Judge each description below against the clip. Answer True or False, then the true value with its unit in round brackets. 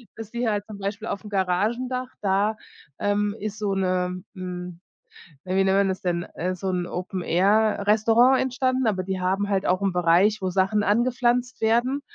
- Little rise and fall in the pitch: False (3.2 semitones)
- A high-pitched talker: True (200 Hz)